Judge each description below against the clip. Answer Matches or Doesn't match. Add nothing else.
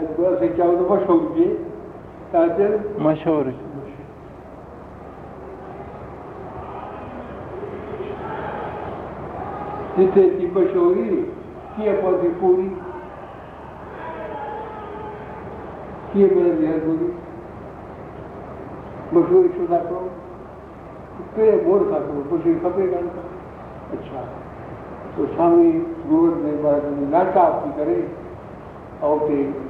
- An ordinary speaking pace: Doesn't match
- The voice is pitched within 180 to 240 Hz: Matches